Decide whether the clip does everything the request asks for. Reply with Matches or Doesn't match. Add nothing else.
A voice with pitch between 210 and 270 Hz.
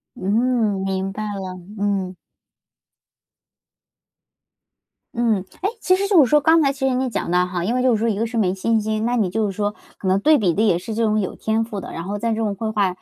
Matches